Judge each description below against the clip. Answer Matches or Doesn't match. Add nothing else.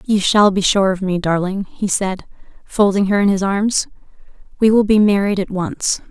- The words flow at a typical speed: Matches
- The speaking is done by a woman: Matches